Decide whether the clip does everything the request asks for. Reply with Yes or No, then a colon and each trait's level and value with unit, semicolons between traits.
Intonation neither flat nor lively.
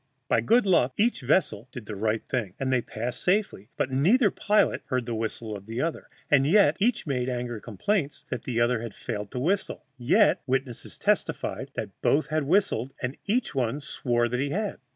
No: wide, 6.6 semitones